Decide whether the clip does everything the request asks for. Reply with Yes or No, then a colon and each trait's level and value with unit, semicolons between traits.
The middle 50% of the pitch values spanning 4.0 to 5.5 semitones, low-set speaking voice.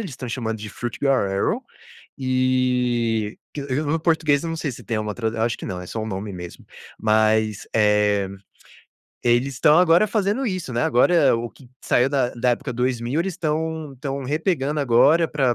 Yes: average, 5.2 semitones; low, 130 Hz